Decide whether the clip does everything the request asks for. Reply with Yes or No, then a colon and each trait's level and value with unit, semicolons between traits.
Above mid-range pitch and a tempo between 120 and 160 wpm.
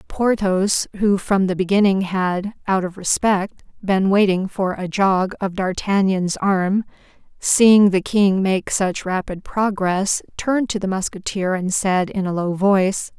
Yes: high, 195 Hz; average, 155 wpm